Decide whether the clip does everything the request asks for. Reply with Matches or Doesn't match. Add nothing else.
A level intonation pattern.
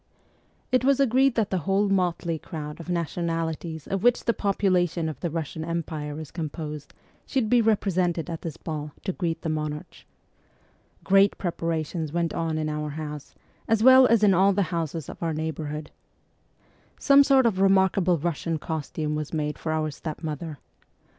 Doesn't match